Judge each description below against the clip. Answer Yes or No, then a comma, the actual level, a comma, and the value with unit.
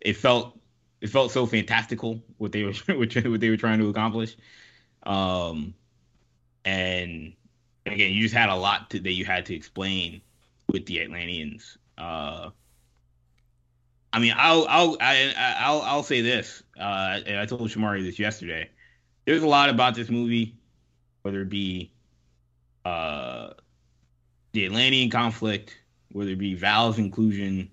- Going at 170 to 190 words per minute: No, average, 145 wpm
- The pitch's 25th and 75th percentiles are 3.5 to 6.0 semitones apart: Yes, average, 4.4 semitones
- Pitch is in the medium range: No, low, 105 Hz